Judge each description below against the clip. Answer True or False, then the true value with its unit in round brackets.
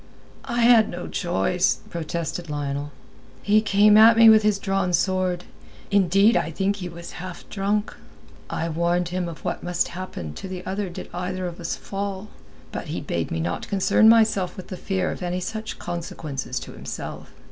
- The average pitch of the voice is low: False (185 Hz)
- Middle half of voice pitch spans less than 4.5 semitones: True (2.9 semitones)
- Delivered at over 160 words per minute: True (180 wpm)